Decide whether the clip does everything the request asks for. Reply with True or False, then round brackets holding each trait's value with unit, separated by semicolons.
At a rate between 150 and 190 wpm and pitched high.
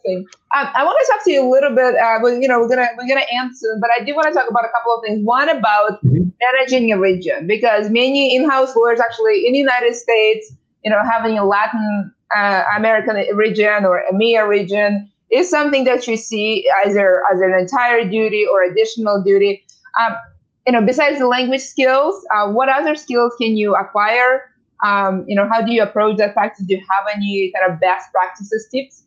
False (205 wpm; 225 Hz)